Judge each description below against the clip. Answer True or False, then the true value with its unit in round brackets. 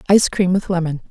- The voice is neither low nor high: True (180 Hz)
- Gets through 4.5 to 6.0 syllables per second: False (7.1 syllables/s)